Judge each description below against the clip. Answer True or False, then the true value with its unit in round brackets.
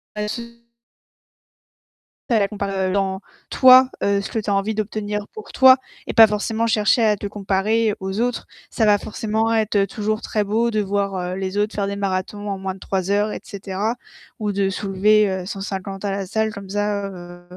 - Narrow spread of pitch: True (1.8 semitones)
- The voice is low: False (205 Hz)